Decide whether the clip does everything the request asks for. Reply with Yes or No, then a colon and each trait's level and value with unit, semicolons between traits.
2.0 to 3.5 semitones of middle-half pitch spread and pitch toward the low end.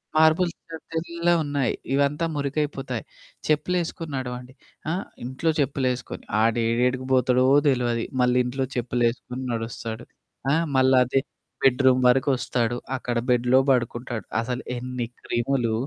Yes: narrow, 2.6 semitones; low, 130 Hz